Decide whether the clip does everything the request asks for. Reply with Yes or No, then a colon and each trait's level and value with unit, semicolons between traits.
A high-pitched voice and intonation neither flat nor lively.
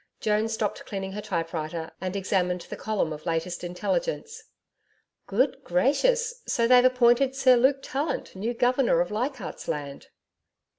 No: high, 220 Hz; wide, 6.5 semitones